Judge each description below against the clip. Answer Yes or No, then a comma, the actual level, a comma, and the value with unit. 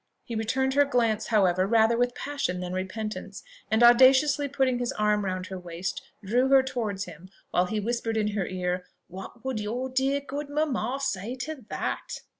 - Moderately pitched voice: No, high, 230 Hz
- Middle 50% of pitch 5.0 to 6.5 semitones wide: Yes, wide, 5.4 semitones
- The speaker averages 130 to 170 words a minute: No, average, 180 wpm